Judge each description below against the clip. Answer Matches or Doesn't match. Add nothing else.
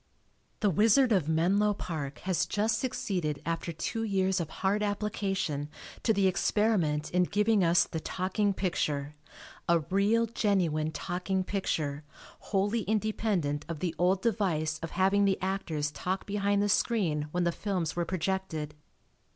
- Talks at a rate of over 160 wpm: Doesn't match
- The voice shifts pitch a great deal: Doesn't match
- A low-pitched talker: Doesn't match